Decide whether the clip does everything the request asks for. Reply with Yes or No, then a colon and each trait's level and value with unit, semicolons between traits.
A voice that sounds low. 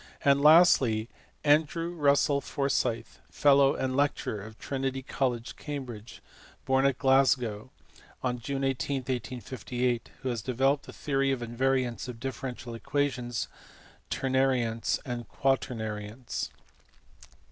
Yes: low, 130 Hz